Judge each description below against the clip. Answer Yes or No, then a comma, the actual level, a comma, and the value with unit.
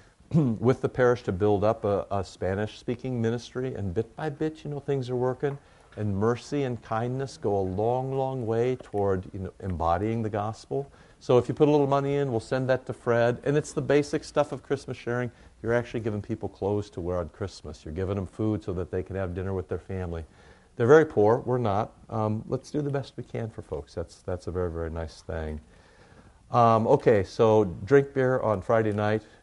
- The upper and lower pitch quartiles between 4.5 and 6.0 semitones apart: Yes, average, 4.8 semitones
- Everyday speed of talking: No, fast, 215 wpm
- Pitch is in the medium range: No, low, 115 Hz